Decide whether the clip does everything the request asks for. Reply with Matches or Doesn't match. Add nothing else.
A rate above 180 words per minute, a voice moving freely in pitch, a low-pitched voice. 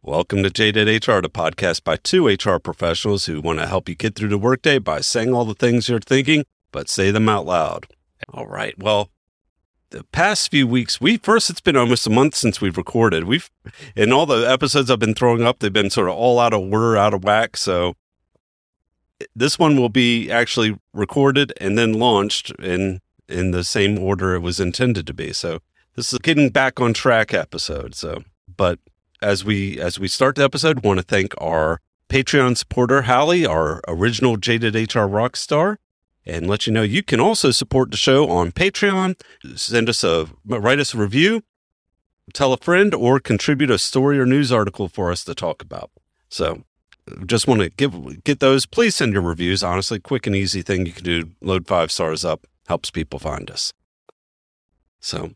Matches